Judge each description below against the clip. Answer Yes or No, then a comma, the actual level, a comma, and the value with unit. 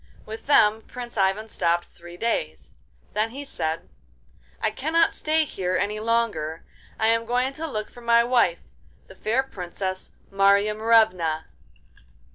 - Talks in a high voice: Yes, high, 215 Hz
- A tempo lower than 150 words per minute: Yes, average, 140 wpm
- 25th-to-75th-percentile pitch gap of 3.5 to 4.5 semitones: Yes, average, 4.2 semitones